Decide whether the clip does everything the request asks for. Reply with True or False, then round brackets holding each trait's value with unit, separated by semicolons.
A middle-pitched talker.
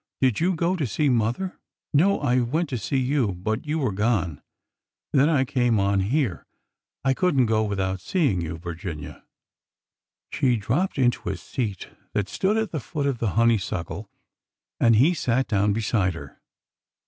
False (115 Hz)